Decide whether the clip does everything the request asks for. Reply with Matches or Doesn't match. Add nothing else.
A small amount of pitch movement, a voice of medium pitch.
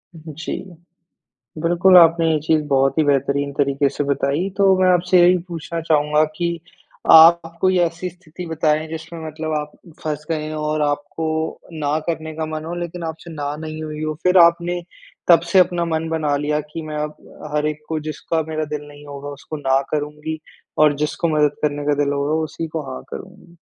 Matches